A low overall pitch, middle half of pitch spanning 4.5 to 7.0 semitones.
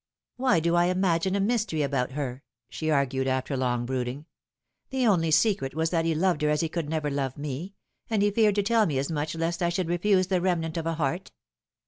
No: medium, 165 Hz; average, 4.8 semitones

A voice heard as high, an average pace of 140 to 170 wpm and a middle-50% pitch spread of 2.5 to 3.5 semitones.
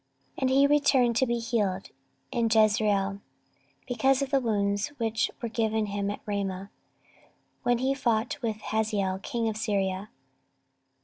Yes: high, 220 Hz; average, 145 wpm; average, 3.1 semitones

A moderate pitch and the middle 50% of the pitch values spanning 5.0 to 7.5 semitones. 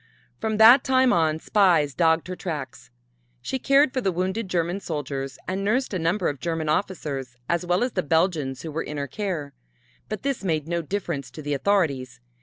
Yes: medium, 170 Hz; average, 5.3 semitones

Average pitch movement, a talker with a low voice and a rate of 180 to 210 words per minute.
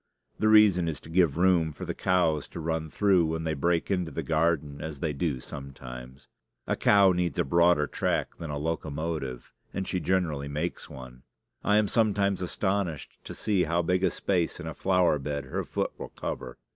Yes: average, 3.9 semitones; very low, 80 Hz; average, 195 wpm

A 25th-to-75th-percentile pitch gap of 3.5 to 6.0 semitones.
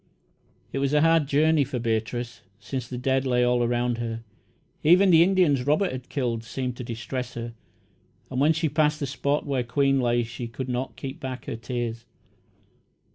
No: average, 3.1 semitones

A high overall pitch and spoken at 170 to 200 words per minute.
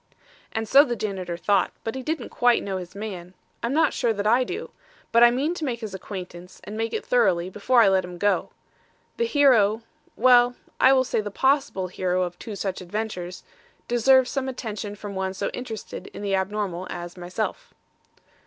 Yes: high, 210 Hz; average, 190 wpm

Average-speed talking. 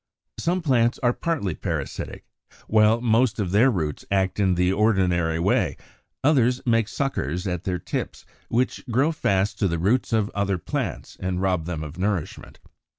Yes: average, 165 wpm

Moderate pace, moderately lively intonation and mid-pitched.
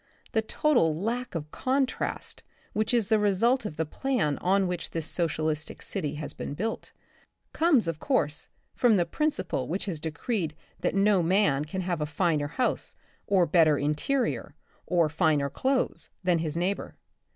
No: average, 160 wpm; wide, 6.0 semitones; medium, 180 Hz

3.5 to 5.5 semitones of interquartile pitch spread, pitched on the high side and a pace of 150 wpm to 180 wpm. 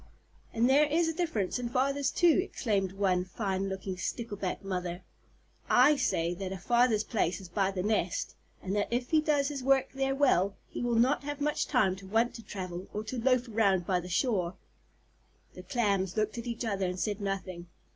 No: average, 5.2 semitones; high, 215 Hz; average, 195 wpm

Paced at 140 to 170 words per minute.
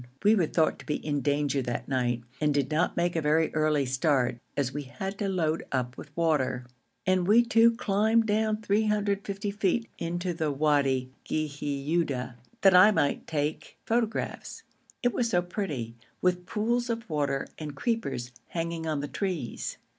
Yes: average, 160 wpm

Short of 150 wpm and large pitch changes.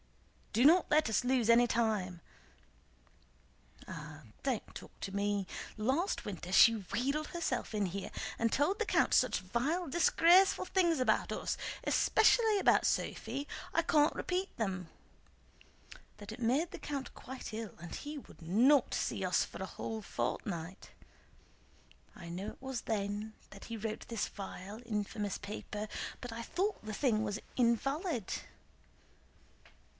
Yes: average, 140 wpm; wide, 6.2 semitones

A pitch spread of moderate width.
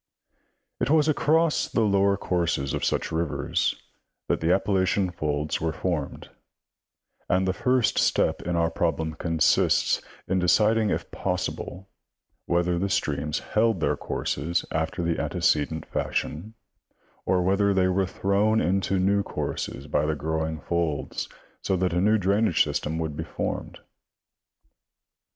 Yes: average, 3.6 semitones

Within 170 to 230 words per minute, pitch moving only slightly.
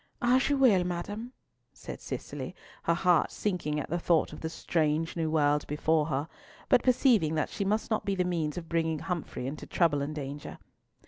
No: average, 190 wpm; average, 4.1 semitones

